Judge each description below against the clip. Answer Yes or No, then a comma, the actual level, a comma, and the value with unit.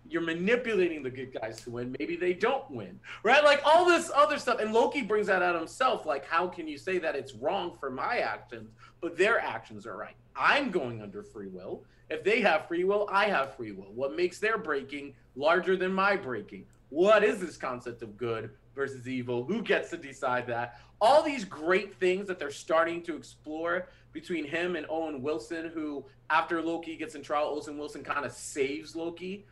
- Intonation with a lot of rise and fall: Yes, wide, 7.1 semitones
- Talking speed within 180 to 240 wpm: Yes, fast, 205 wpm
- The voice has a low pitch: No, medium, 165 Hz